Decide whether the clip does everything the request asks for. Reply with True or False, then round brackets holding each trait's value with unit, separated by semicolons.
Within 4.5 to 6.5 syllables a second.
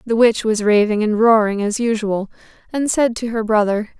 True (5.0 syllables/s)